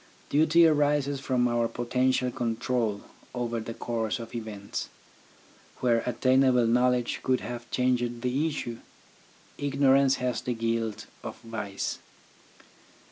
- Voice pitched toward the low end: Yes, low, 125 Hz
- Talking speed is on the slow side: Yes, slow, 115 wpm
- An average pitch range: No, narrow, 2.2 semitones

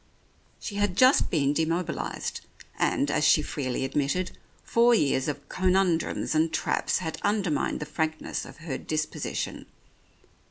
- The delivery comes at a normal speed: No, slow, 130 wpm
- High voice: No, medium, 160 Hz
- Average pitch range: Yes, average, 3.9 semitones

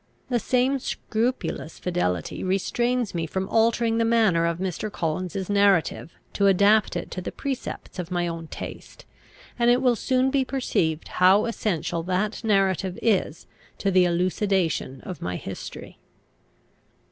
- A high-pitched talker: Yes, high, 195 Hz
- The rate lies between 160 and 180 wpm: No, average, 145 wpm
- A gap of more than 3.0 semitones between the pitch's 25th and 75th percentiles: Yes, average, 4.7 semitones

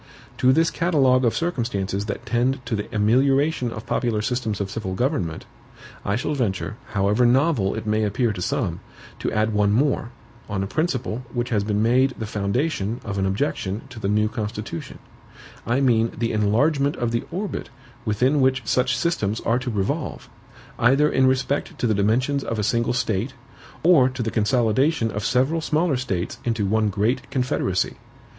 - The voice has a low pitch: Yes, low, 115 Hz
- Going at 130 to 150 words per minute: No, average, 175 wpm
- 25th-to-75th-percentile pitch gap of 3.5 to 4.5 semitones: Yes, average, 4.0 semitones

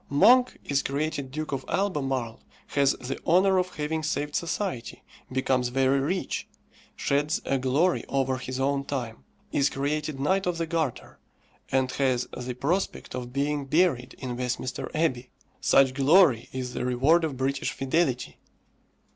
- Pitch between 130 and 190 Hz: Yes, medium, 140 Hz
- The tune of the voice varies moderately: Yes, average, 3.4 semitones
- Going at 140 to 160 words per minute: Yes, average, 145 wpm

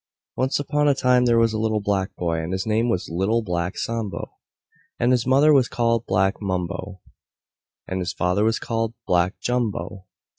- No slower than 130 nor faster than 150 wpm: No, average, 180 wpm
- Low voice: Yes, low, 110 Hz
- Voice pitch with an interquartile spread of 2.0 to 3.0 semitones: No, average, 4.2 semitones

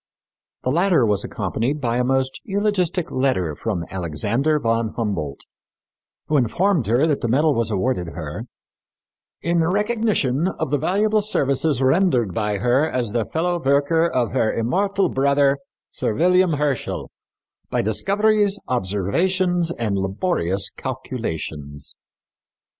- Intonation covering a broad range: Yes, wide, 7.9 semitones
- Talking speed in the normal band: No, slow, 125 wpm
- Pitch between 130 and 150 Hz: Yes, low, 135 Hz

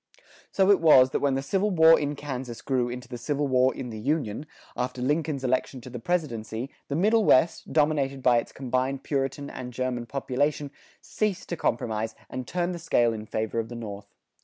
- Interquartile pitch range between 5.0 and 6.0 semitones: No, average, 3.7 semitones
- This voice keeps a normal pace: Yes, average, 195 wpm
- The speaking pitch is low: Yes, low, 130 Hz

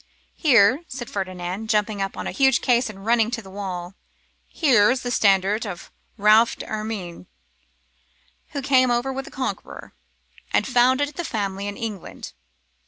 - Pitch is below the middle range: No, high, 220 Hz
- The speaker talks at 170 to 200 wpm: No, average, 150 wpm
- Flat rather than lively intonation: No, average, 4.3 semitones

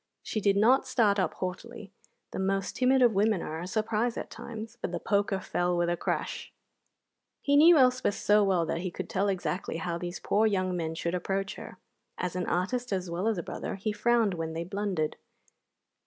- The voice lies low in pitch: No, high, 195 Hz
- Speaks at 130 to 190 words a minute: No, average, 200 wpm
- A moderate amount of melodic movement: Yes, average, 3.9 semitones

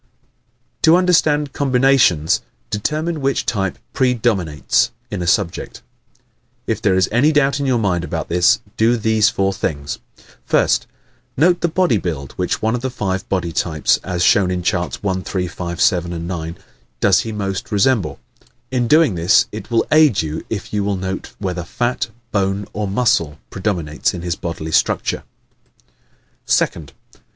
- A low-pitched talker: Yes, low, 100 Hz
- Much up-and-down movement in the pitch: Yes, wide, 6.0 semitones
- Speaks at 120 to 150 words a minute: No, average, 160 wpm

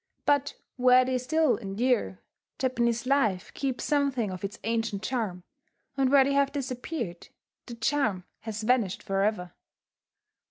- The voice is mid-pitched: No, high, 245 Hz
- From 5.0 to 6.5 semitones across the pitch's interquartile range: No, average, 4.5 semitones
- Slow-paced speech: Yes, slow, 130 wpm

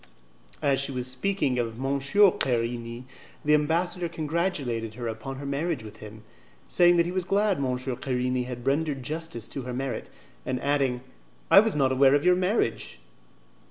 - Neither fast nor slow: Yes, average, 165 wpm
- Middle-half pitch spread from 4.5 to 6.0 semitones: Yes, average, 4.9 semitones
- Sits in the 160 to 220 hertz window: No, low, 135 Hz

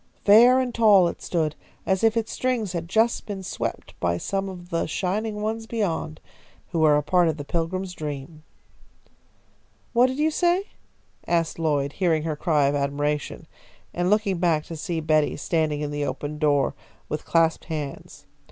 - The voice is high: No, medium, 170 Hz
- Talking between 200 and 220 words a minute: No, average, 170 wpm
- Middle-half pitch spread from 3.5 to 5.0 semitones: No, wide, 5.4 semitones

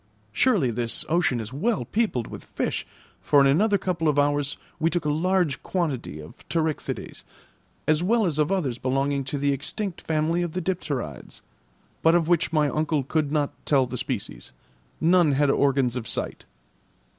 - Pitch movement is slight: No, average, 4.1 semitones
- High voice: No, medium, 150 Hz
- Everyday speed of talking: Yes, average, 170 wpm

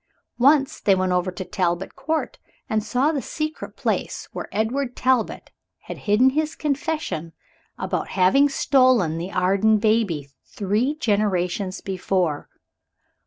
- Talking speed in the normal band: No, slow, 125 wpm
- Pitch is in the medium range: No, high, 215 Hz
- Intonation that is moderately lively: No, wide, 6.4 semitones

